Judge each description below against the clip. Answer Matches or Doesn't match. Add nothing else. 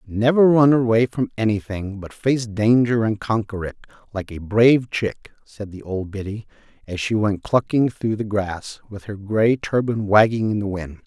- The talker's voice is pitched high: Doesn't match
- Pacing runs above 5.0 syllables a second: Doesn't match